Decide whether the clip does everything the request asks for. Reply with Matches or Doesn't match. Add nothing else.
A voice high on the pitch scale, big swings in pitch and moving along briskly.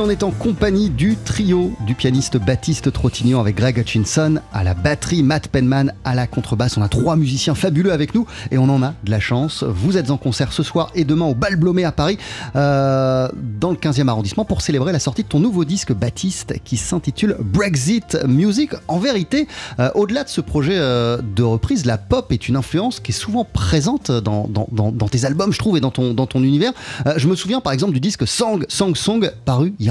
Doesn't match